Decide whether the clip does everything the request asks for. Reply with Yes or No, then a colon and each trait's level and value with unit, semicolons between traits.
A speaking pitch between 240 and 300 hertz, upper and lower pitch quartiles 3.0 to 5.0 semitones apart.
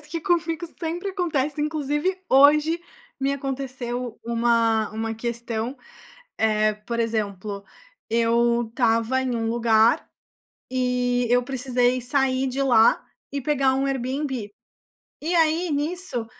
Yes: very high, 255 Hz; average, 3.9 semitones